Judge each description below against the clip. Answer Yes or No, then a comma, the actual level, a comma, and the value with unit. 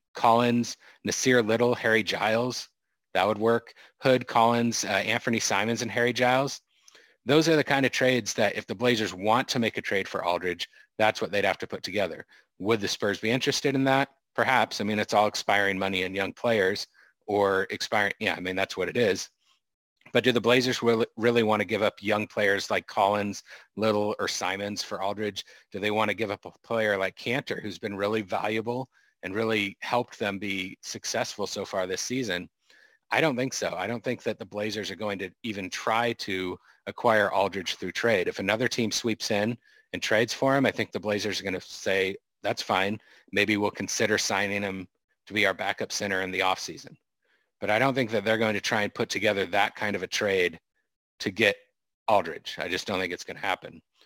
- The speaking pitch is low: Yes, low, 110 Hz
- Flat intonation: No, average, 3.3 semitones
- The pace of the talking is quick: Yes, fast, 210 wpm